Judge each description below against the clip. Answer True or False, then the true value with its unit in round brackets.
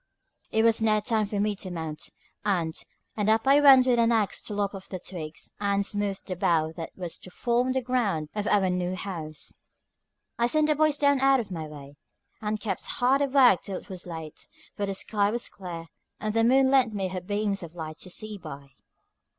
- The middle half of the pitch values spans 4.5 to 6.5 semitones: True (4.8 semitones)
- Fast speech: True (215 wpm)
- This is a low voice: False (205 Hz)